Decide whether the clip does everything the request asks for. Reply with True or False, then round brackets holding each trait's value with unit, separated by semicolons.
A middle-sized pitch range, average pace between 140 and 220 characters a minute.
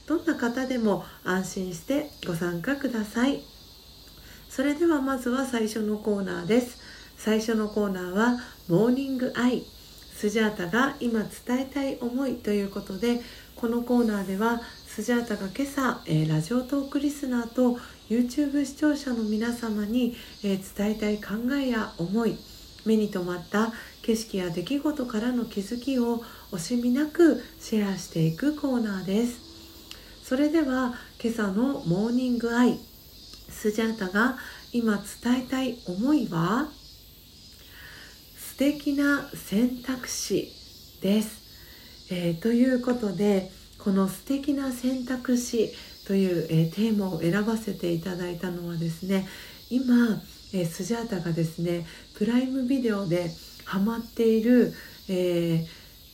False (4.3 semitones; 265 characters per minute)